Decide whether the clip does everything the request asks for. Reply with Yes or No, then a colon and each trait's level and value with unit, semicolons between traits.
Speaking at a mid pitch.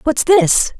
No: very high, 285 Hz